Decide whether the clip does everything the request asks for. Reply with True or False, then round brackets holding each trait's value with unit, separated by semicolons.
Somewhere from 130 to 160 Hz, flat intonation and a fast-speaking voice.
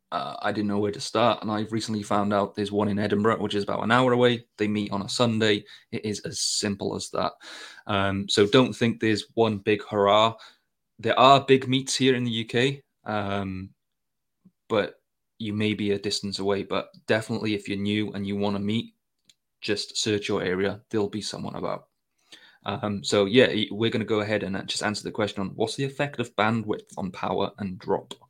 False (105 Hz; 2.0 semitones; 210 wpm)